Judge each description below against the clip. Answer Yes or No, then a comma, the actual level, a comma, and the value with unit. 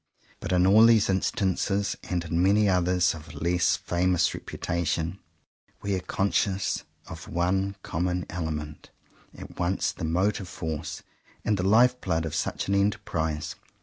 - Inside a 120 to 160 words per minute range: Yes, average, 150 wpm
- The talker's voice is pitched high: No, very low, 90 Hz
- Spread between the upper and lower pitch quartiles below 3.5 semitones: Yes, average, 3.0 semitones